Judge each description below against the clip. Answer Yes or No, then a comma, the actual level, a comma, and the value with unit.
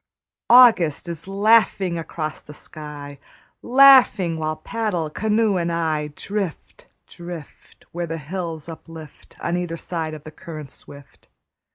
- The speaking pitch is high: No, medium, 170 Hz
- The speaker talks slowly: Yes, slow, 130 wpm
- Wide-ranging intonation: No, average, 3.8 semitones